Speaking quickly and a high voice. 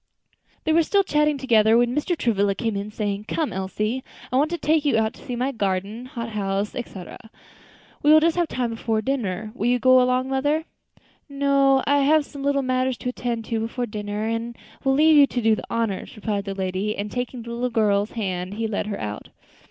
Yes: fast, 215 wpm; high, 235 Hz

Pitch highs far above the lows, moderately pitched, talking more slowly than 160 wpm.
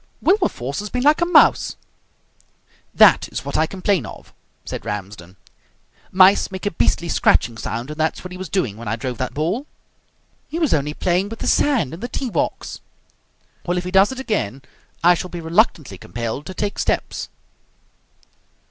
No: wide, 7.6 semitones; medium, 175 Hz; average, 180 wpm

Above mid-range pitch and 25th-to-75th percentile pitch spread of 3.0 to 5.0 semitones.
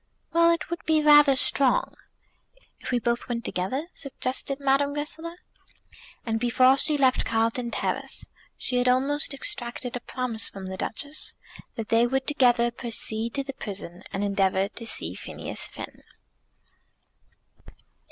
Yes: very high, 250 Hz; average, 3.8 semitones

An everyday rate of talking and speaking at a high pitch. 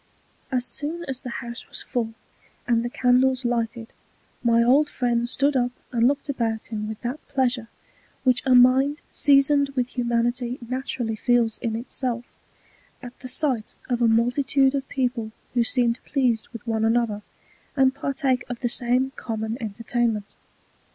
Yes: average, 160 wpm; high, 245 Hz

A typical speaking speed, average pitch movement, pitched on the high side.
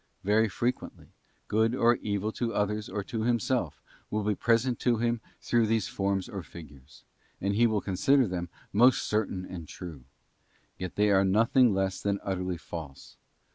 No: average, 170 wpm; average, 3.8 semitones; low, 105 Hz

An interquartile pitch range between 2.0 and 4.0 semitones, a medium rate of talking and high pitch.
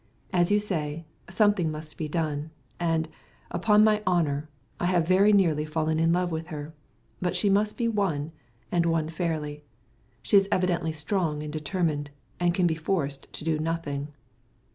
No: average, 3.2 semitones; average, 165 wpm; medium, 165 Hz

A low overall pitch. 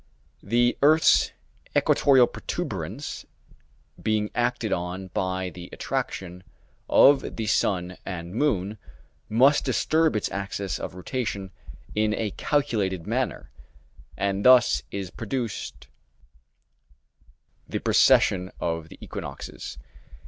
Yes: low, 100 Hz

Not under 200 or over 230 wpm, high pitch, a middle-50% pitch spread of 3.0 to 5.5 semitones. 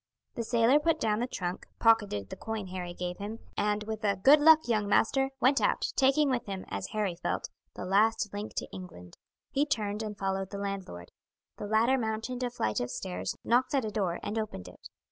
Yes: fast, 205 wpm; high, 215 Hz; average, 3.9 semitones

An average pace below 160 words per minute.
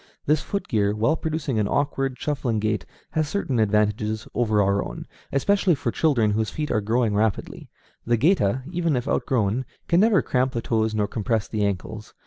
No: average, 180 wpm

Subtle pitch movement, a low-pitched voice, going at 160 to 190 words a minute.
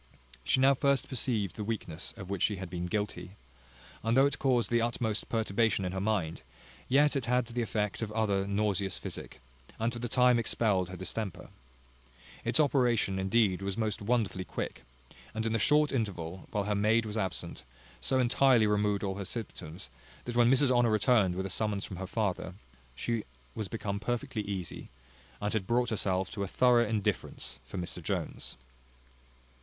No: average, 3.6 semitones; low, 105 Hz; average, 175 wpm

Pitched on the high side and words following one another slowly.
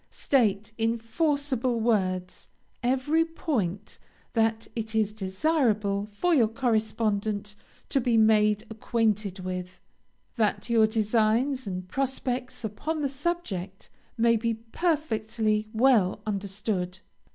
Yes: high, 220 Hz; slow, 105 wpm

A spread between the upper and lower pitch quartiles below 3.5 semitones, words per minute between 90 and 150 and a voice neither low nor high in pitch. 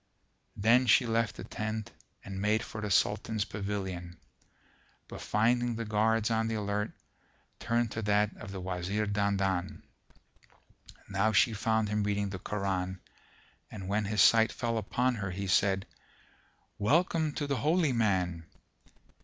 No: narrow, 2.5 semitones; average, 145 wpm; low, 105 Hz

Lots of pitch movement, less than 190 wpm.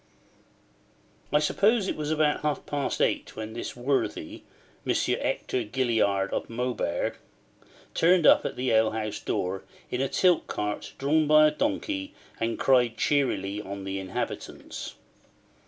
Yes: wide, 6.0 semitones; average, 140 wpm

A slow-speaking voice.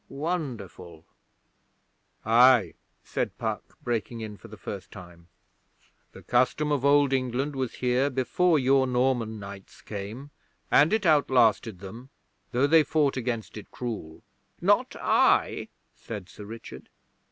Yes: slow, 130 wpm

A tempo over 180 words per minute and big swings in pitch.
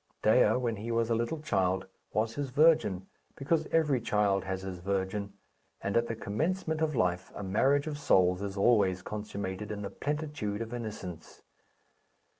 No: average, 165 wpm; wide, 6.2 semitones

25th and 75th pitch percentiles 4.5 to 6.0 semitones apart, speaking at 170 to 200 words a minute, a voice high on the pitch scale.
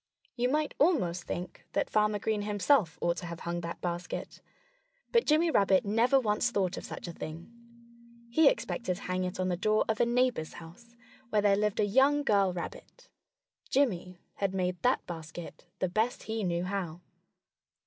Yes: average, 5.1 semitones; average, 180 wpm; high, 200 Hz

